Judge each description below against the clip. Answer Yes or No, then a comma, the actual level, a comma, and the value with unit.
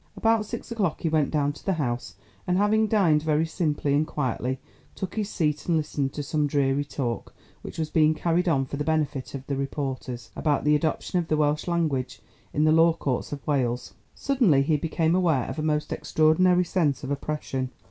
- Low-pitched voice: No, medium, 150 Hz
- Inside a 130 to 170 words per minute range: No, average, 200 wpm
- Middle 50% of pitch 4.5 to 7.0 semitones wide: No, average, 3.1 semitones